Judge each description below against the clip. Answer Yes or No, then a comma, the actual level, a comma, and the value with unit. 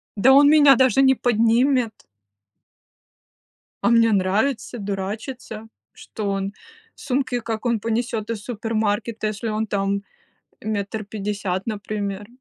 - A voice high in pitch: Yes, high, 220 Hz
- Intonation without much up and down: No, average, 3.0 semitones